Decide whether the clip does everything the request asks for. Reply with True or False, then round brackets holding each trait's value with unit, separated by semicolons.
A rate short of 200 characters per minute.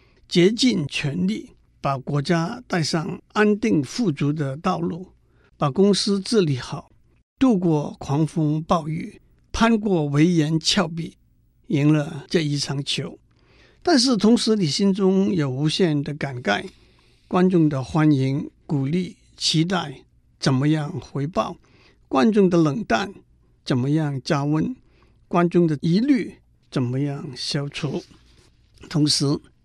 True (180 characters per minute)